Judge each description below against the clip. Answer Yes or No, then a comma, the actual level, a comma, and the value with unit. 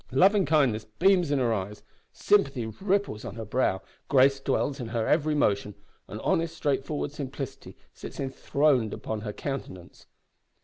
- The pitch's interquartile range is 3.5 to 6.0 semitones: Yes, average, 5.3 semitones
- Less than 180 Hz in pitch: Yes, low, 135 Hz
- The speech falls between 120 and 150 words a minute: Yes, average, 145 wpm